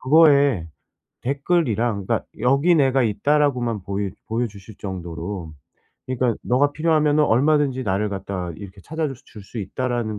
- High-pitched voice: No, low, 120 Hz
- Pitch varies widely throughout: Yes, wide, 6.1 semitones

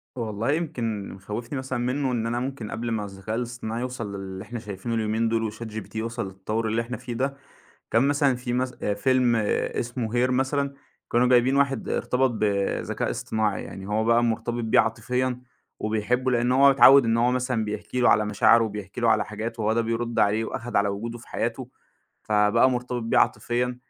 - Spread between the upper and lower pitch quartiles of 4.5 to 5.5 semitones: No, narrow, 2.6 semitones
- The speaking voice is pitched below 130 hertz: Yes, low, 115 Hz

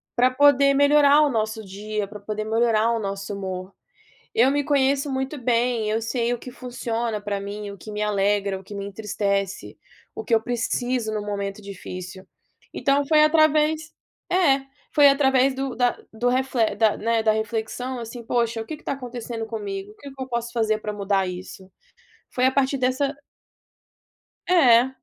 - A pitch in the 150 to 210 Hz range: No, high, 230 Hz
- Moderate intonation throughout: Yes, average, 4.2 semitones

